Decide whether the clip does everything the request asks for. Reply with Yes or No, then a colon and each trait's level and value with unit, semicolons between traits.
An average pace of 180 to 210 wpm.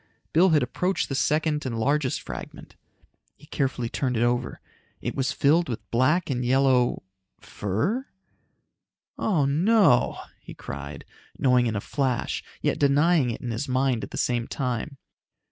No: average, 150 wpm